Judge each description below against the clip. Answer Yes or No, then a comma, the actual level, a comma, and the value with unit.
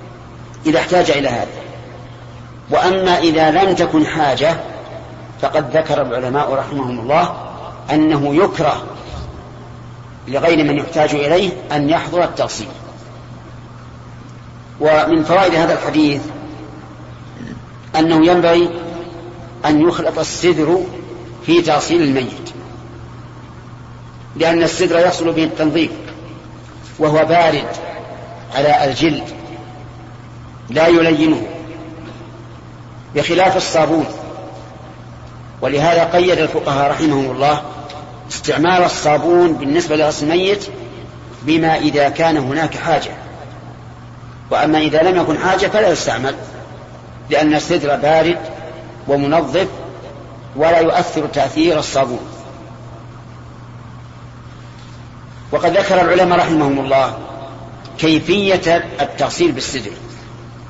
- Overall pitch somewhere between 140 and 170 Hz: Yes, medium, 155 Hz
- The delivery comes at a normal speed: Yes, average, 85 wpm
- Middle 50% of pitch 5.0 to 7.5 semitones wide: No, average, 4.2 semitones